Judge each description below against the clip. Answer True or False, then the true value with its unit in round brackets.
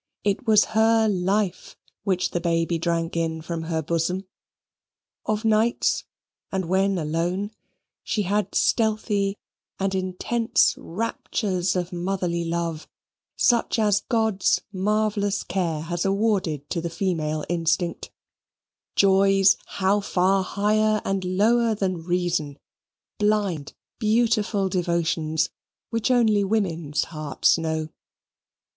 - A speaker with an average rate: False (110 wpm)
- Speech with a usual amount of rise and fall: True (3.7 semitones)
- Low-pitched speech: False (190 Hz)